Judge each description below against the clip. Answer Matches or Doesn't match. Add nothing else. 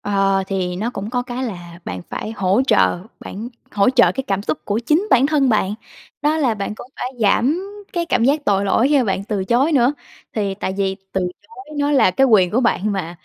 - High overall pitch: Matches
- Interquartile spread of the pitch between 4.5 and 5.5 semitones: Matches